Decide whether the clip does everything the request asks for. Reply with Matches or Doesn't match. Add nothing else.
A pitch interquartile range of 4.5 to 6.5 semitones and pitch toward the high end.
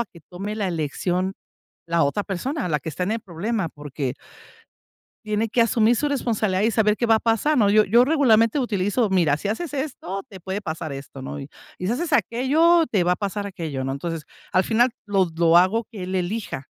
Matches